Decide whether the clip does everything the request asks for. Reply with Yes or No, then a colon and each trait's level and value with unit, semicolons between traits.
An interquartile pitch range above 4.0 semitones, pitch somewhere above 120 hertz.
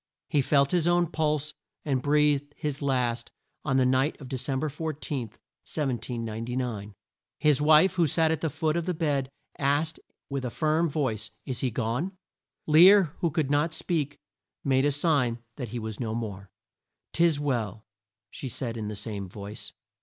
Yes: average, 4.4 semitones; medium, 140 Hz